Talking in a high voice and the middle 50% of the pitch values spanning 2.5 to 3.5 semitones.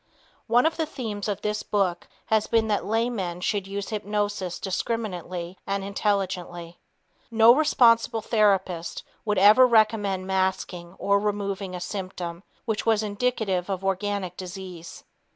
Yes: high, 200 Hz; average, 2.8 semitones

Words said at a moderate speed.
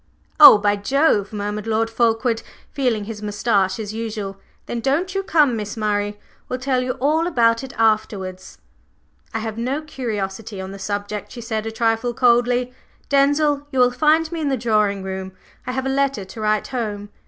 Yes: average, 180 wpm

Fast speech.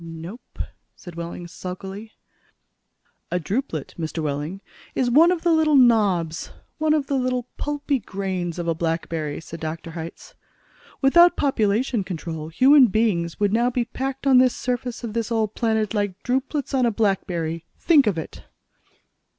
No: average, 155 wpm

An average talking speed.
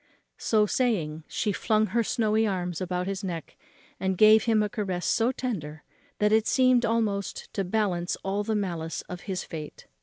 Yes: average, 175 wpm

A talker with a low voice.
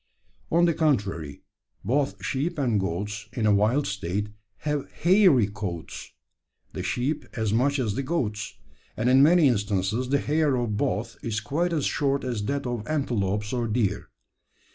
Yes: low, 120 Hz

